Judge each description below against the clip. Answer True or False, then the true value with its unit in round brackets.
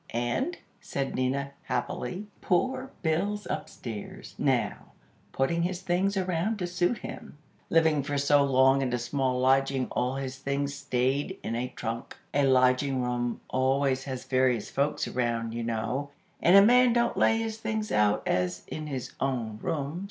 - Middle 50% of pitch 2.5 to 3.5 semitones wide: False (5.5 semitones)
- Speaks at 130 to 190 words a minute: True (160 wpm)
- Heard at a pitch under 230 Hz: True (135 Hz)